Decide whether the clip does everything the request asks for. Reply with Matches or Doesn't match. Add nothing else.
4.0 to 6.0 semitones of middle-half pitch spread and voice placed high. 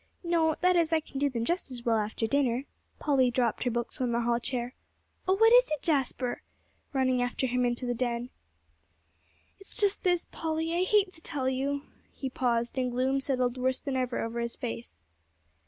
Matches